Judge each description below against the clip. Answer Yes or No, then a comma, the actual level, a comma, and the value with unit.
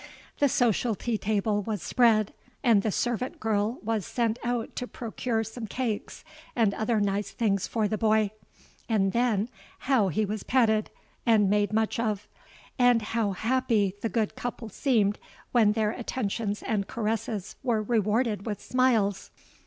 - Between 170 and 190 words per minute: No, average, 150 wpm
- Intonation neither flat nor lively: No, narrow, 2.3 semitones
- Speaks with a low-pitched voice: No, high, 220 Hz